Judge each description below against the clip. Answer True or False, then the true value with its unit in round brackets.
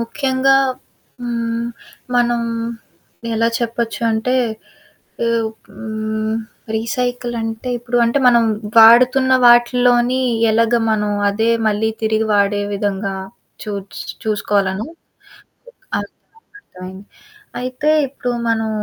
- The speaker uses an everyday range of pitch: False (2.0 semitones)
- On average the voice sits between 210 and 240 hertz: True (230 Hz)